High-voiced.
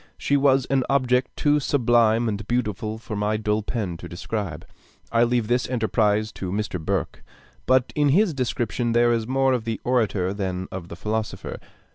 No: low, 115 Hz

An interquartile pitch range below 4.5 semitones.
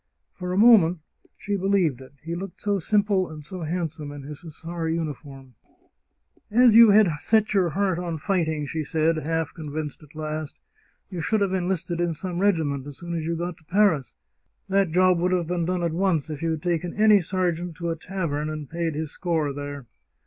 Yes: average, 3.2 semitones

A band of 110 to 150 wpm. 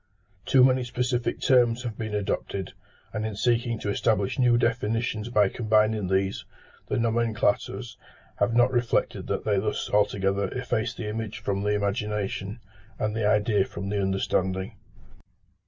Yes: average, 145 wpm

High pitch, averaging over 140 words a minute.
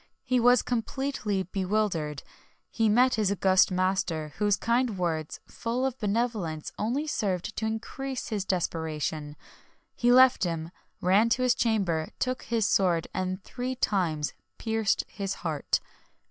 No: high, 205 Hz; slow, 135 wpm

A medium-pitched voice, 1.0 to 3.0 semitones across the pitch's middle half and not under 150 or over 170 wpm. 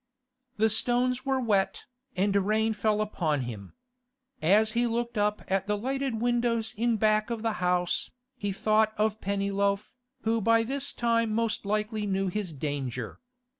No: high, 215 Hz; narrow, 2.6 semitones; average, 160 wpm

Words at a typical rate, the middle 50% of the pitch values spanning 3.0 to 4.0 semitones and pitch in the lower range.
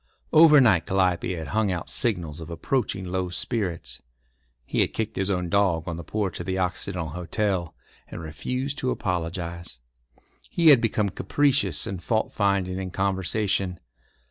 Yes: average, 155 wpm; average, 3.6 semitones; very low, 95 Hz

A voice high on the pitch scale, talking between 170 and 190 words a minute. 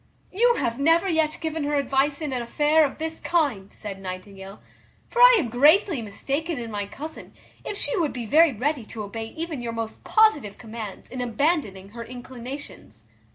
Yes: very high, 270 Hz; average, 180 wpm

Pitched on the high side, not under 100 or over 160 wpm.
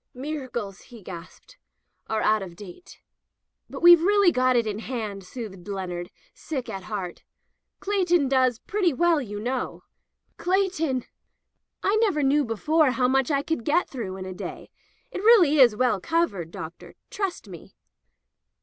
Yes: very high, 255 Hz; average, 155 wpm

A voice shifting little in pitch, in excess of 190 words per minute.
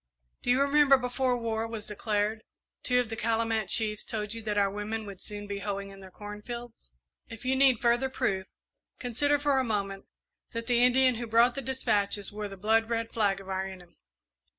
No: average, 3.1 semitones; average, 200 wpm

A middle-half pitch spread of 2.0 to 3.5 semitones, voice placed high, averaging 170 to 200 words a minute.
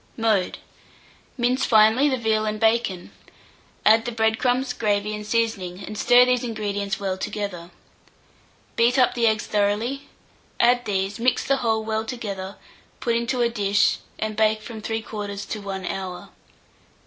No: average, 2.7 semitones; high, 220 Hz; average, 150 wpm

